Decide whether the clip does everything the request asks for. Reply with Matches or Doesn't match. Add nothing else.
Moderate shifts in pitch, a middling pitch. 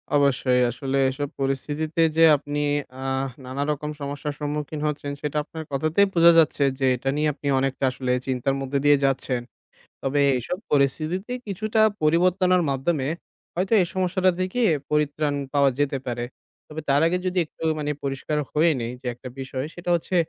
Matches